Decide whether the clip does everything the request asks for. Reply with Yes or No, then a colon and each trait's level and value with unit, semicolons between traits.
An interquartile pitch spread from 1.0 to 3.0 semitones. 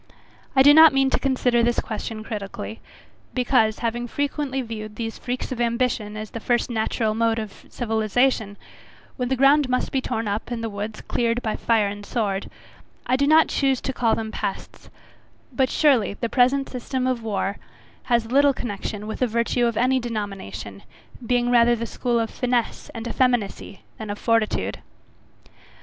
Yes: average, 2.7 semitones